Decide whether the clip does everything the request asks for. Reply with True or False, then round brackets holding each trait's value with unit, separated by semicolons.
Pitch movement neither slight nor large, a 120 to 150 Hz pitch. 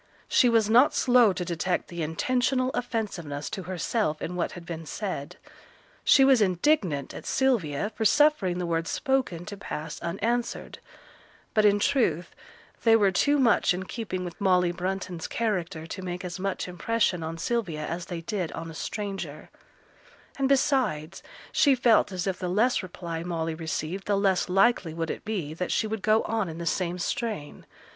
False (5.0 semitones; 185 Hz)